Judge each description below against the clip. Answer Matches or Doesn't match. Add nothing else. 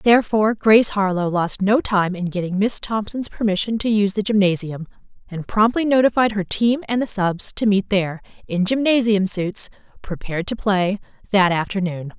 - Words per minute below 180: Matches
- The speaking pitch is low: Doesn't match